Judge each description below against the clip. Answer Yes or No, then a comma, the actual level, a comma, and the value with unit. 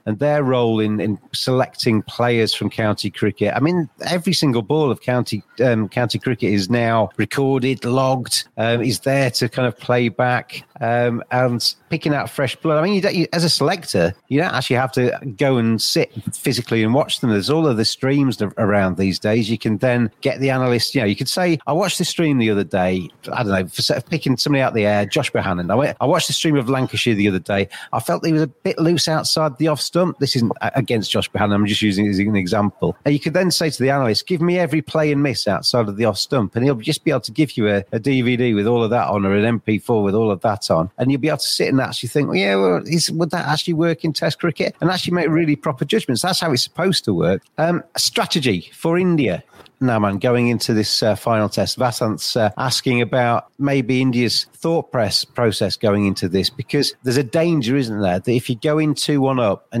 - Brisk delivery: Yes, fast, 245 wpm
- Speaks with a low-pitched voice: Yes, low, 125 Hz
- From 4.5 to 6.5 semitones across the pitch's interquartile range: Yes, wide, 5.5 semitones